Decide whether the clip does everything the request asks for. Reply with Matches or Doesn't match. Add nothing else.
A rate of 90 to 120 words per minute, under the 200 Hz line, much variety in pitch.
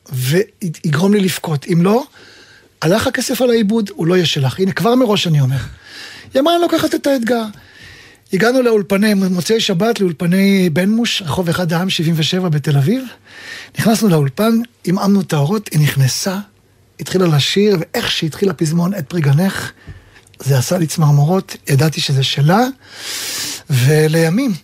Doesn't match